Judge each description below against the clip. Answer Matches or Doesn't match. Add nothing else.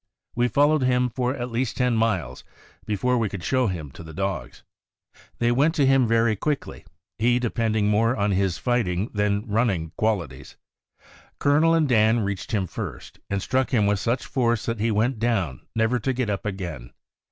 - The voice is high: Doesn't match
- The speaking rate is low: Doesn't match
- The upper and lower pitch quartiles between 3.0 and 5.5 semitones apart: Matches